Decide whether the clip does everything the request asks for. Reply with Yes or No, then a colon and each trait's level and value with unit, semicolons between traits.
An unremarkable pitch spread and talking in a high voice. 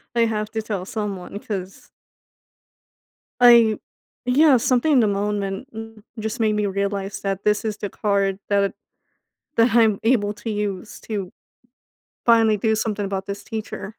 No: narrow, 2.2 semitones; high, 210 Hz